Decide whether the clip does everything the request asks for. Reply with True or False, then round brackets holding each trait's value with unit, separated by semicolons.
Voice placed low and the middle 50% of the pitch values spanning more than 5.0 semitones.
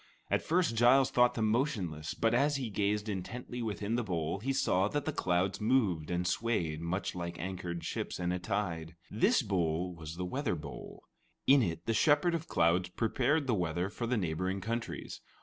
True (100 Hz; 5.6 semitones)